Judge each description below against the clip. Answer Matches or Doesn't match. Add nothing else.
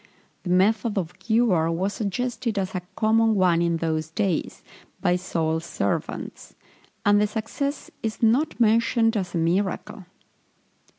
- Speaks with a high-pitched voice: Matches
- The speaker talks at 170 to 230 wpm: Doesn't match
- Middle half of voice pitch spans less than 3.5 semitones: Doesn't match